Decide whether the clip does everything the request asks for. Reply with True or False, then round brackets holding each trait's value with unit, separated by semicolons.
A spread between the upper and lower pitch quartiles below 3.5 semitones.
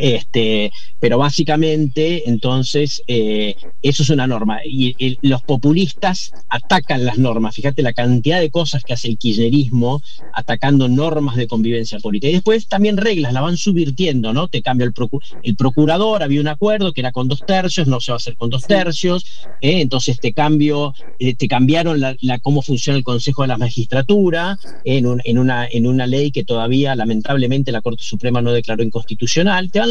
False (4.1 semitones)